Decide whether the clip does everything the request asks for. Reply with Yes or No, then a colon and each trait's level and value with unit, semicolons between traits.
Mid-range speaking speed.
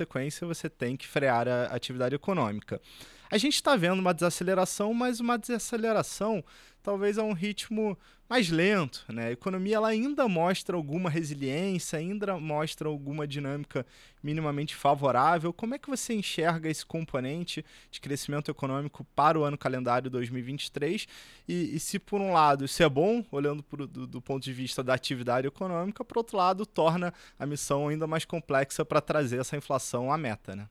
Yes: average, 170 wpm